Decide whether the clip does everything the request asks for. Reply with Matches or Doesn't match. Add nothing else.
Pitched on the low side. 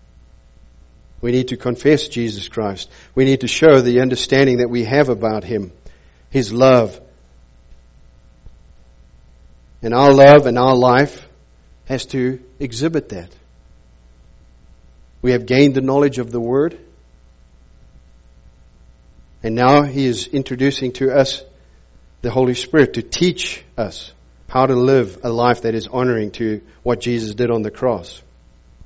Matches